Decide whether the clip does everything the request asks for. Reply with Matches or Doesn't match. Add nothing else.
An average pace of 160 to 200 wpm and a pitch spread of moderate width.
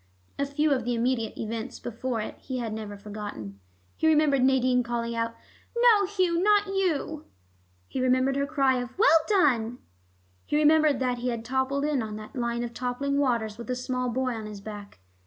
Matches